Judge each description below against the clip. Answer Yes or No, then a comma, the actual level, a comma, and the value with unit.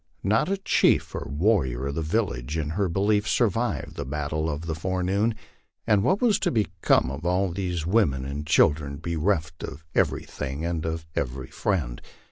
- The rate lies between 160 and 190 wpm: Yes, average, 175 wpm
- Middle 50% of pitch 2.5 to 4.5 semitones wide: No, wide, 5.6 semitones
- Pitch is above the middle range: No, very low, 80 Hz